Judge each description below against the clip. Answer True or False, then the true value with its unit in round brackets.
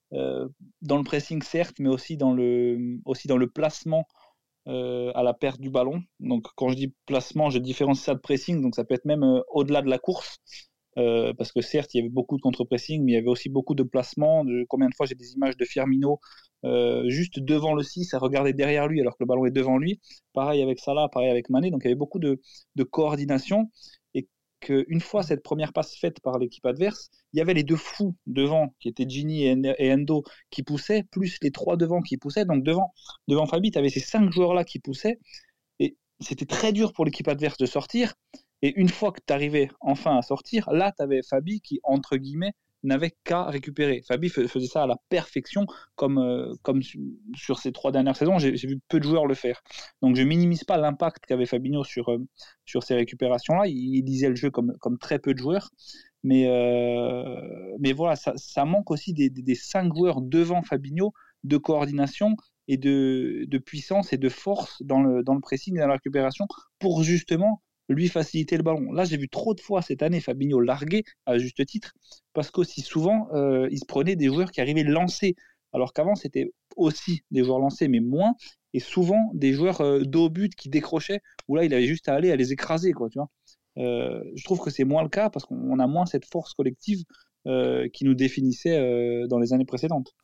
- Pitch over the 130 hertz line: True (140 Hz)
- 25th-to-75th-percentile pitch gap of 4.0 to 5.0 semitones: True (4.7 semitones)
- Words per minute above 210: True (220 wpm)